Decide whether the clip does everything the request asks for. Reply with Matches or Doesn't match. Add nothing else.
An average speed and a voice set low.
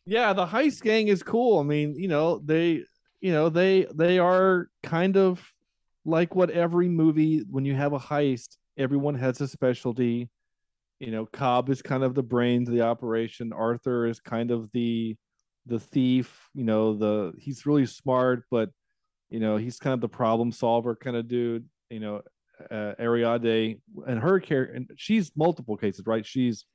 Matches